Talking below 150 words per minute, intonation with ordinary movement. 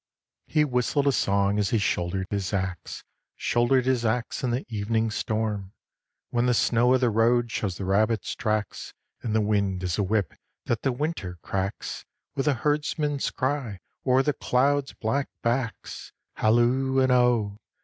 No: average, 165 wpm; average, 4.1 semitones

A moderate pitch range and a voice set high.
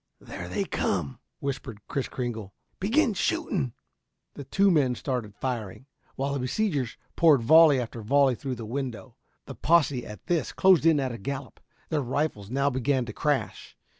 No: average, 4.1 semitones; low, 135 Hz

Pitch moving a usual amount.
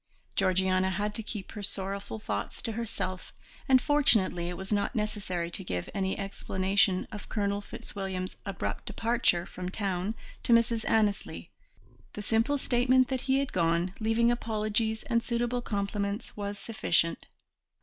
Yes: average, 3.3 semitones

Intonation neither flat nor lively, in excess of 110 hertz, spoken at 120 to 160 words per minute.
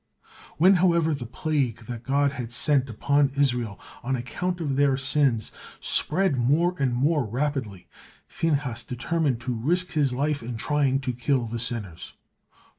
Yes: average, 3.7 semitones; low, 135 Hz; average, 150 wpm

